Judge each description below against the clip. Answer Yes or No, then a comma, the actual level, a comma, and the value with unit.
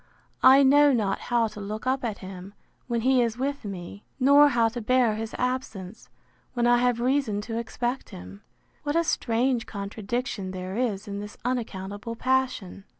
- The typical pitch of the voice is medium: No, high, 235 Hz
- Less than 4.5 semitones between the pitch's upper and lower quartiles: Yes, average, 4.0 semitones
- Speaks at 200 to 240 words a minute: No, average, 170 wpm